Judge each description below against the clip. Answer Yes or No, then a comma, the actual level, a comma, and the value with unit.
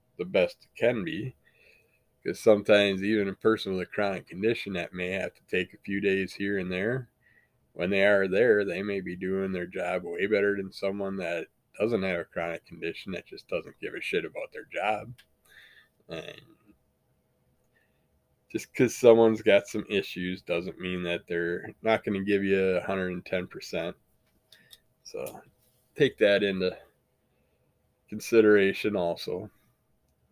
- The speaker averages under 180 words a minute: Yes, average, 150 wpm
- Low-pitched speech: Yes, low, 100 Hz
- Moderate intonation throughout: Yes, average, 3.1 semitones